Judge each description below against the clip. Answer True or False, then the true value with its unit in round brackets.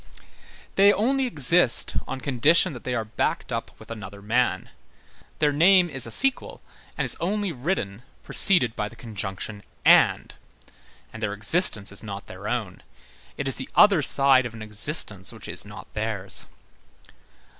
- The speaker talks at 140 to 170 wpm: True (155 wpm)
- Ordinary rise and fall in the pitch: False (7.8 semitones)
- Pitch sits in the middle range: False (125 Hz)